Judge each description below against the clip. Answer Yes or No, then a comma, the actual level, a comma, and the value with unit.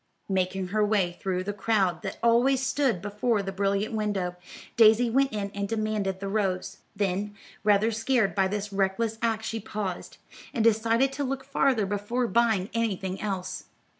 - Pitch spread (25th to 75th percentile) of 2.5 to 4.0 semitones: Yes, average, 2.9 semitones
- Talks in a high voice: Yes, high, 210 Hz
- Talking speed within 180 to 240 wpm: No, average, 165 wpm